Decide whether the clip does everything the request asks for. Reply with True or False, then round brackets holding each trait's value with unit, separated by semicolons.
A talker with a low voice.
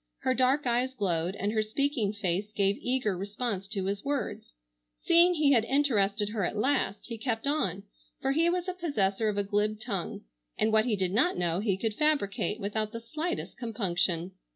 False (215 Hz)